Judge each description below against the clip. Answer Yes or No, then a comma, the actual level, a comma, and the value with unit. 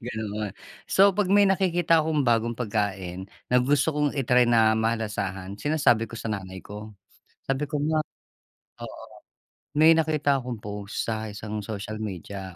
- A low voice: Yes, low, 115 Hz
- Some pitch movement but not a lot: No, wide, 6.0 semitones